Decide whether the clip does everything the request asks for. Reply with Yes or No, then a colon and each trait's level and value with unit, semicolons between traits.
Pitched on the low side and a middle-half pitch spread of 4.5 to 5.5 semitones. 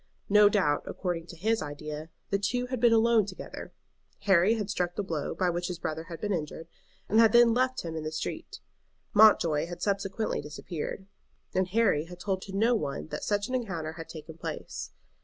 No: high, 190 Hz; average, 5.0 semitones